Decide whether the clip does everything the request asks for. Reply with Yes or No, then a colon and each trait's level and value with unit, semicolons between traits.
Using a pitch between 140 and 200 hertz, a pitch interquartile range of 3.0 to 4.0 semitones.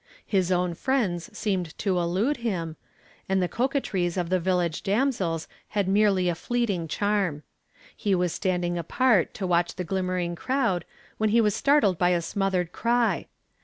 Yes: medium, 185 Hz; average, 3.4 semitones